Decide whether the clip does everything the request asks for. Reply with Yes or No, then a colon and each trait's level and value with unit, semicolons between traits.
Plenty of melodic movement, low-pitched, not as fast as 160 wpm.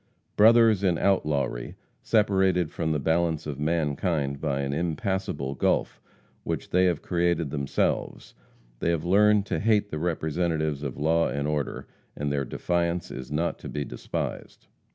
No: average, 3.9 semitones; very low, 80 Hz; average, 150 wpm